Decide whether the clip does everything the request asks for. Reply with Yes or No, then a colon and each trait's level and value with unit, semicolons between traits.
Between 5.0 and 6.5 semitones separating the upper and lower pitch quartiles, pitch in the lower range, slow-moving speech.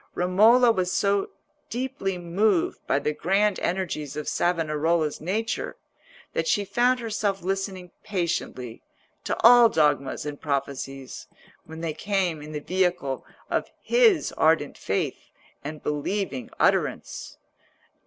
No: average, 5.3 semitones; medium, 180 Hz; slow, 120 wpm